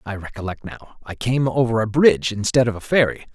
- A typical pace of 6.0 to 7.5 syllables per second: Yes, 6.1 syllables/s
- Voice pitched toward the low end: Yes, low, 115 Hz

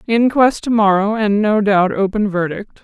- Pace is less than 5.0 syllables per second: Yes, 4.5 syllables/s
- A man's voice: No, female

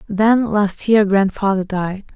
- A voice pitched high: Yes, high, 200 Hz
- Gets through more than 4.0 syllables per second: No, 3.7 syllables/s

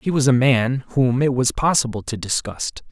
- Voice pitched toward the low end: Yes, low, 125 Hz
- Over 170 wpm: Yes, fast, 205 wpm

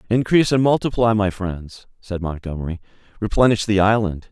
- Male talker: Yes, male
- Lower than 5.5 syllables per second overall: No, 5.6 syllables/s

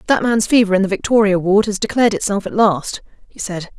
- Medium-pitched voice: No, high, 205 Hz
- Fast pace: Yes, fast, 220 wpm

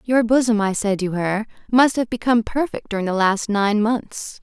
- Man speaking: No, female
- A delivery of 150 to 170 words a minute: No, fast, 205 wpm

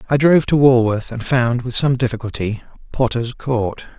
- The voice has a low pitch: Yes, low, 125 Hz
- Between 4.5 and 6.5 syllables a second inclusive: Yes, 5.0 syllables/s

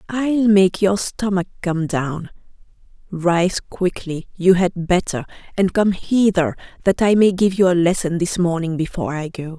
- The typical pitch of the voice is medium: Yes, medium, 180 Hz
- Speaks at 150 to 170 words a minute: Yes, average, 165 wpm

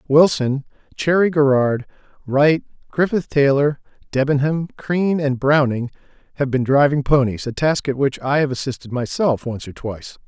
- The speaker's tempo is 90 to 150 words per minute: Yes, average, 145 wpm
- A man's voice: Yes, male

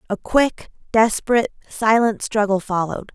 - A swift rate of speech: No, slow, 115 wpm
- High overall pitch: Yes, high, 215 Hz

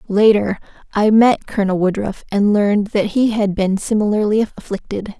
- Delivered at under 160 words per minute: Yes, average, 150 wpm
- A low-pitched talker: No, high, 205 Hz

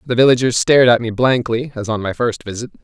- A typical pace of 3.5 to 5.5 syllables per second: No, 6.2 syllables/s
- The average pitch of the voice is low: Yes, low, 120 Hz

